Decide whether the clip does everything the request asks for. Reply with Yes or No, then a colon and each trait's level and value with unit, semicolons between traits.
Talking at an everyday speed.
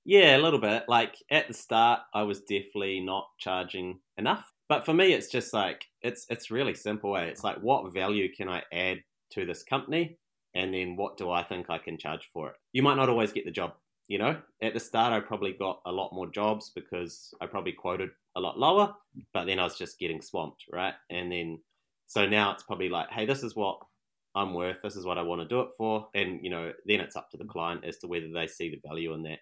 No: fast, 245 wpm